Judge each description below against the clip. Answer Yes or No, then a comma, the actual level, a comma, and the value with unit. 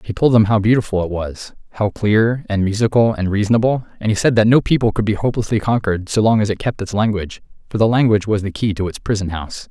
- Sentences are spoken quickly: Yes, fast, 245 wpm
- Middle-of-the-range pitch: No, low, 105 Hz